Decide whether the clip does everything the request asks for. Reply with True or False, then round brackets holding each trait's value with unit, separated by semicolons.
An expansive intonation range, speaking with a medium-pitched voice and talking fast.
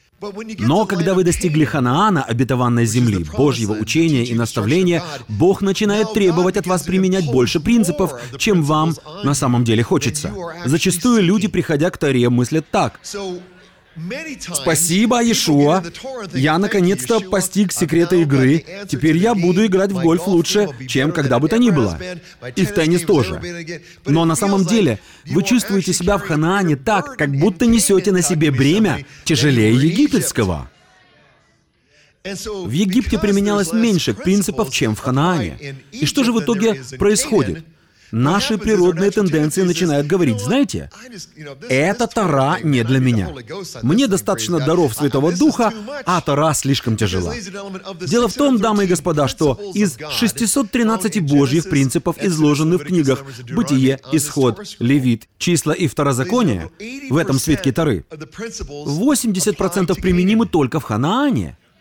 False (6.0 semitones; 175 Hz; 135 wpm)